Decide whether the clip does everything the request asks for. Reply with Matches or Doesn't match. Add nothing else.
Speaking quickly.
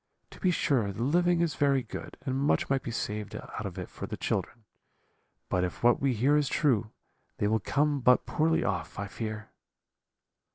Doesn't match